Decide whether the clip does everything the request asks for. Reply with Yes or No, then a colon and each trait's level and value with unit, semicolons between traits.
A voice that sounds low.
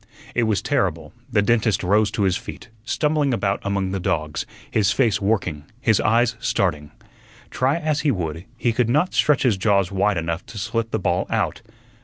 Yes: low, 105 Hz